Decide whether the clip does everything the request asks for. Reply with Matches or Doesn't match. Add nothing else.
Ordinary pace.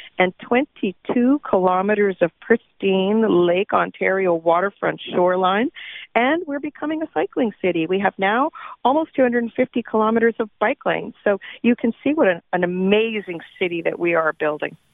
Matches